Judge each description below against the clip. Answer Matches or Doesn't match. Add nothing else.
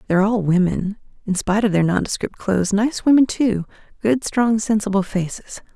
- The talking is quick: Doesn't match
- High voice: Matches